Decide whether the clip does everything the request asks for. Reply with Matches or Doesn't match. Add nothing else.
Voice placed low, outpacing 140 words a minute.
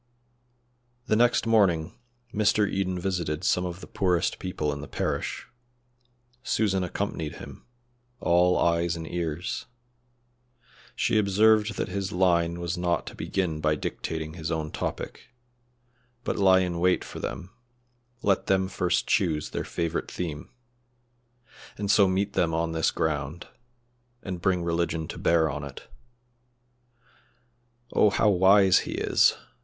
Doesn't match